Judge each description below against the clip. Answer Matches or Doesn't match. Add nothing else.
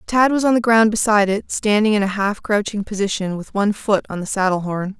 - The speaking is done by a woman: Matches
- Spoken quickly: Matches